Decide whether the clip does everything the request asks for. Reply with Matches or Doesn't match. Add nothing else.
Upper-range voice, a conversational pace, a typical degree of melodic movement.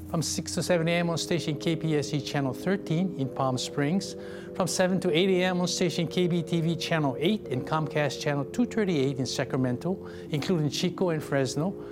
Doesn't match